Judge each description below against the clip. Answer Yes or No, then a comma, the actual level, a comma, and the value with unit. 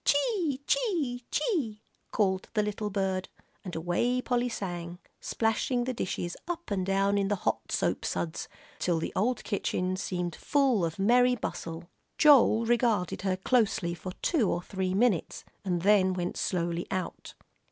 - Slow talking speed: No, average, 150 wpm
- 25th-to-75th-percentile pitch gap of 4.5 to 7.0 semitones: Yes, average, 5.3 semitones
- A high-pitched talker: Yes, high, 200 Hz